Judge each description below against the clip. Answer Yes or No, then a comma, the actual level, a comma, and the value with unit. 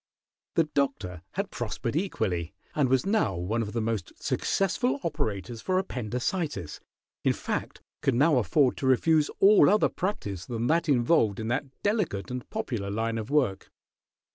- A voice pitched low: Yes, low, 125 Hz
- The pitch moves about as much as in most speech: No, wide, 7.1 semitones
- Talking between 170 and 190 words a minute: No, average, 155 wpm